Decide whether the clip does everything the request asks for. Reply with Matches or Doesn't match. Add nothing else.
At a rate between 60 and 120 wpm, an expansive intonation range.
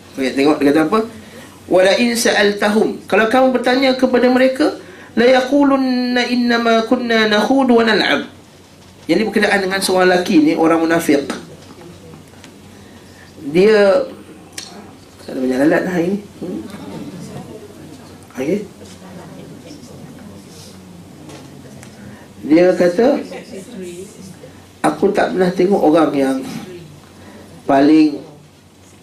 Matches